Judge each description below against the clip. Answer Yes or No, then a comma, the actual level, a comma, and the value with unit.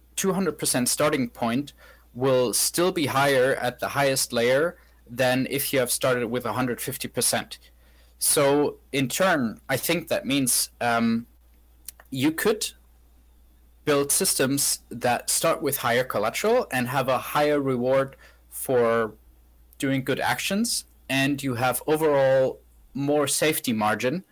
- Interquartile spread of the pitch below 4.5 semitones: No, average, 5.1 semitones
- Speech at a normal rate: No, slow, 125 wpm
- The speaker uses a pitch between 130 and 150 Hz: Yes, low, 135 Hz